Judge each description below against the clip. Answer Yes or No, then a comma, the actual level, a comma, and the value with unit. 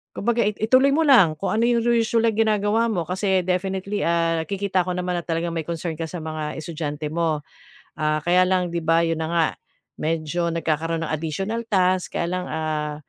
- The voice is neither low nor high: Yes, medium, 175 Hz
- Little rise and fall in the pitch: No, average, 3.7 semitones